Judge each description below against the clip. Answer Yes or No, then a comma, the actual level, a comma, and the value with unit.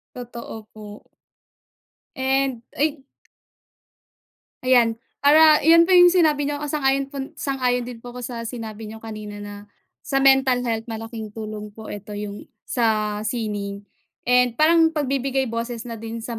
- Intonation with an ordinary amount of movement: Yes, average, 3.7 semitones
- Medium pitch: No, high, 245 Hz